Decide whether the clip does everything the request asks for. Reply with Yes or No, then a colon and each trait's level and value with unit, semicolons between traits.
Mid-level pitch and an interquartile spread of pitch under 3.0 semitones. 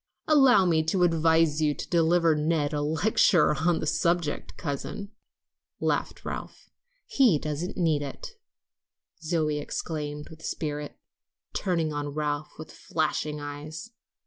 Yes: medium, 155 Hz; narrow, 2.4 semitones